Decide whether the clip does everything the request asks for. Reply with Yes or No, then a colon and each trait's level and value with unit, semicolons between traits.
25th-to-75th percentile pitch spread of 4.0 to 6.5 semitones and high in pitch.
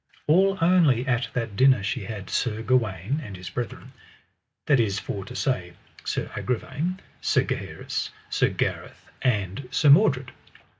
No: average, 5.1 semitones; low, 125 Hz